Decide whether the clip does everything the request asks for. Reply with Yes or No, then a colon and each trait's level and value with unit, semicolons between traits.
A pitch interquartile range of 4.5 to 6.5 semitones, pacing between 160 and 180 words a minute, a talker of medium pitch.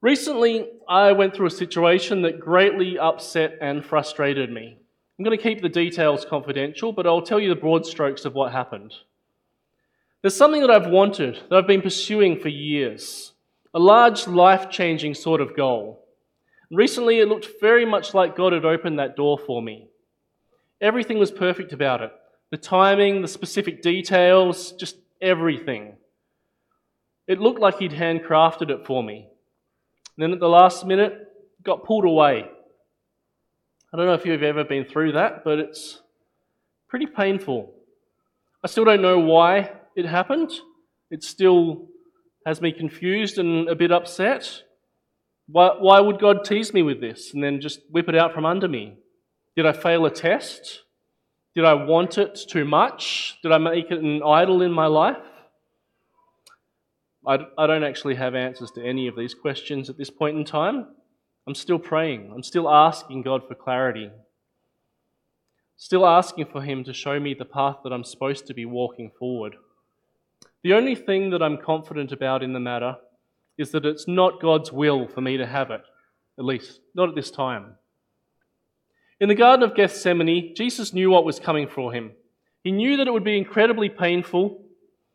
Yes: average, 5.3 semitones; average, 170 wpm; medium, 170 Hz